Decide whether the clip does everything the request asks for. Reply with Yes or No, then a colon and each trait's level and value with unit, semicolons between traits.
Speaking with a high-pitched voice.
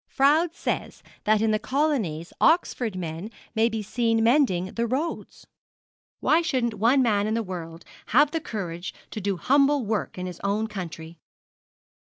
Yes: high, 220 Hz